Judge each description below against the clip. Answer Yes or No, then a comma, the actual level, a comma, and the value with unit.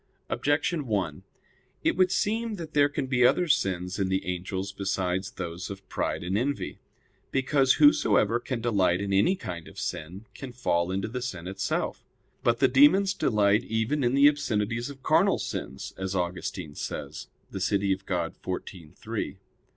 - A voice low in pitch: Yes, low, 105 Hz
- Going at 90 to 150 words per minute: No, average, 165 wpm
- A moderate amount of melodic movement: No, wide, 6.3 semitones